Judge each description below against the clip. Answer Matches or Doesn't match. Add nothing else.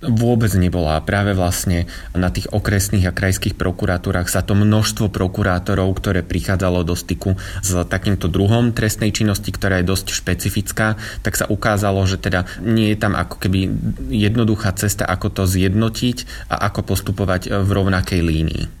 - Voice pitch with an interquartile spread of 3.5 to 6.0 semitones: Doesn't match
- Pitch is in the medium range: Doesn't match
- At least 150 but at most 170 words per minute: Matches